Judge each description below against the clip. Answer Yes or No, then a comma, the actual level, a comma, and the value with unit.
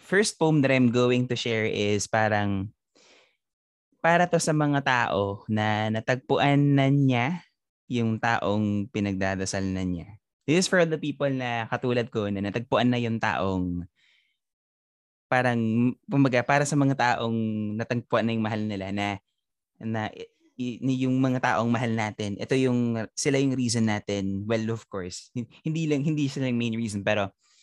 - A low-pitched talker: Yes, low, 115 Hz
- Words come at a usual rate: No, fast, 160 wpm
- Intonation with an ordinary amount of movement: Yes, average, 4.2 semitones